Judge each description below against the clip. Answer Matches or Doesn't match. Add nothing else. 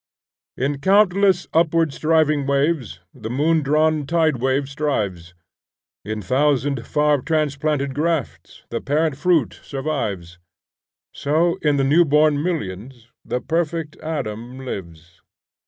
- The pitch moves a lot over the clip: Doesn't match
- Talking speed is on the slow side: Matches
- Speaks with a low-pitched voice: Doesn't match